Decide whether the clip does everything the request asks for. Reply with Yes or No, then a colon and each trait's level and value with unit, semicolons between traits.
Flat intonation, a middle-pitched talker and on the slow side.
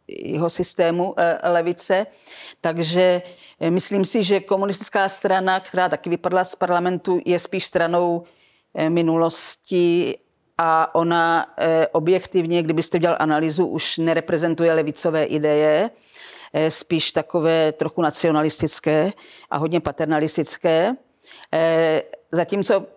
Yes: narrow, 2.0 semitones; medium, 170 Hz; slow, 95 wpm